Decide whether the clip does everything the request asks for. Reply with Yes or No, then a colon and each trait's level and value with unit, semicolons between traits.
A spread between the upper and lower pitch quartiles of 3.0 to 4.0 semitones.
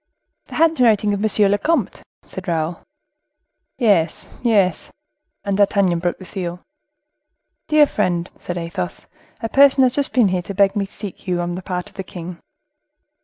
Yes: average, 3.7 semitones